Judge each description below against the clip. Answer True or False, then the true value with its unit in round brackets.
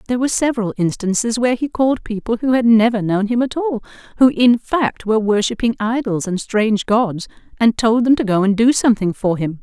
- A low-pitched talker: False (225 Hz)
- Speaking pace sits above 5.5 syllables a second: True (5.8 syllables/s)